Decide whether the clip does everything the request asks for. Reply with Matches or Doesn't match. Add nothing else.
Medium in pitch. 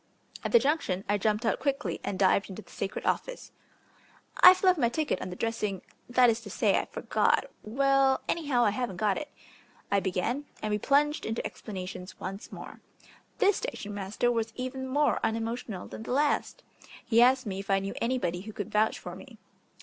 Doesn't match